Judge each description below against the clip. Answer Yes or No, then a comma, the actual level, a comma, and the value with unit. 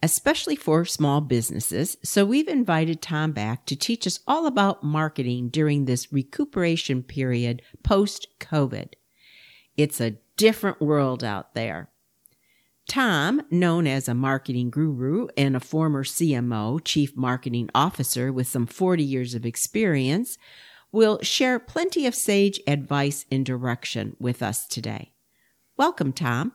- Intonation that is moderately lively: No, wide, 5.8 semitones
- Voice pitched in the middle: Yes, medium, 145 Hz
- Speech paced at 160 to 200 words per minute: No, slow, 135 wpm